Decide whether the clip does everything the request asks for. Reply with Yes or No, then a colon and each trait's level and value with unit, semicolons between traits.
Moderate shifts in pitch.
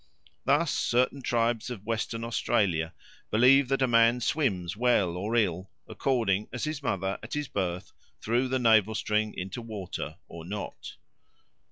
Yes: average, 4.2 semitones